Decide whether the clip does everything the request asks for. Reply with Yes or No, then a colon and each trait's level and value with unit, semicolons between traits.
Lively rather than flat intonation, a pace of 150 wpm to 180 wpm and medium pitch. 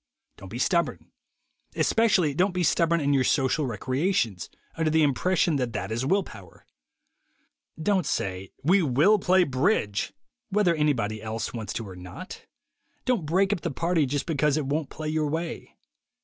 Yes: wide, 6.0 semitones; average, 165 wpm; medium, 150 Hz